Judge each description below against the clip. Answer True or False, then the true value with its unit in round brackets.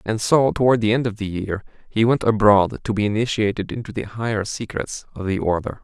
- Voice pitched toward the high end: False (110 Hz)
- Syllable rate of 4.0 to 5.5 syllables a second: False (5.7 syllables/s)